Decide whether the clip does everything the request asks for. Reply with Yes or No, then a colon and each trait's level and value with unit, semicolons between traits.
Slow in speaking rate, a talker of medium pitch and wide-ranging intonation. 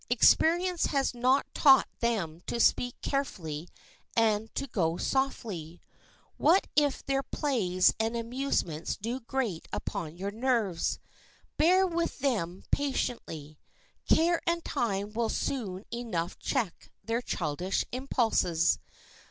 No: slow, 115 wpm; high, 230 Hz; wide, 7.0 semitones